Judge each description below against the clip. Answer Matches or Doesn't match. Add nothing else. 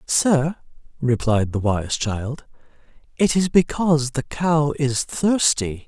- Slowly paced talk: Matches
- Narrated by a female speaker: Doesn't match